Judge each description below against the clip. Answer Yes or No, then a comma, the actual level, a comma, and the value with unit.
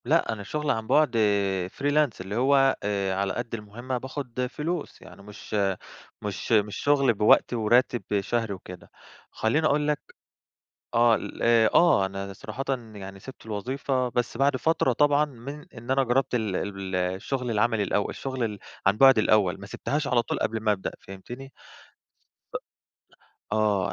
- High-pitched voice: No, low, 115 Hz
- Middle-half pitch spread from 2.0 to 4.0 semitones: No, average, 4.7 semitones